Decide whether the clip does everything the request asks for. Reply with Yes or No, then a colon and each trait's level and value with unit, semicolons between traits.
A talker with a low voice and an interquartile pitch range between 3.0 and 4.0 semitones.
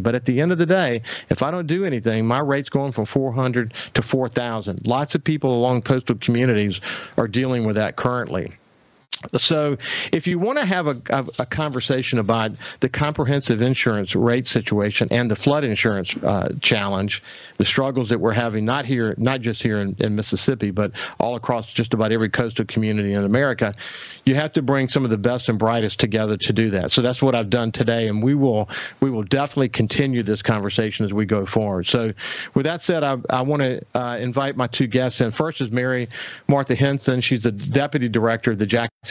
Yes: low, 120 Hz; average, 3.3 semitones